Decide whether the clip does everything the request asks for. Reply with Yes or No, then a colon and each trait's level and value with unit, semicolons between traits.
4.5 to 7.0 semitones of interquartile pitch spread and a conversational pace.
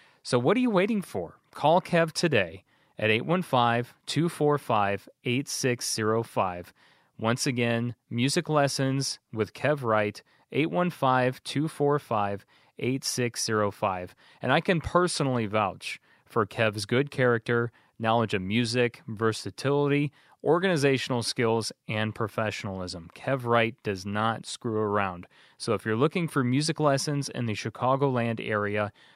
No: average, 4.8 semitones; slow, 115 wpm